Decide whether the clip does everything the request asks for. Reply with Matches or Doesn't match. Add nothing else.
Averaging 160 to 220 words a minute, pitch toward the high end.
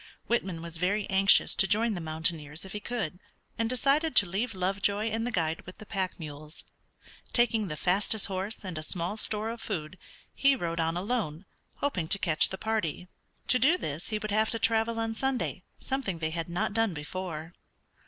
Matches